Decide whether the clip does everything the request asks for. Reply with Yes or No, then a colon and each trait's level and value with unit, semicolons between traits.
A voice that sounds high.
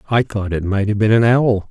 No: low, 105 Hz